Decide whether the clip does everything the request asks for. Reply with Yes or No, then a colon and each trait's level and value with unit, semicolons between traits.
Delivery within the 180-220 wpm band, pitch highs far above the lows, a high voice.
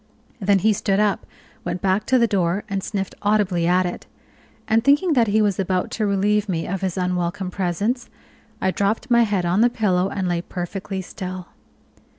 No: average, 185 wpm; average, 2.7 semitones; high, 195 Hz